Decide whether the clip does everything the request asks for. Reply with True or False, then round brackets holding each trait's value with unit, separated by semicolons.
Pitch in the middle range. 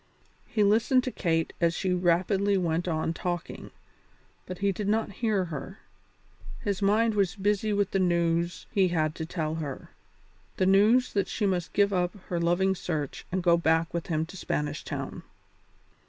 True (180 Hz)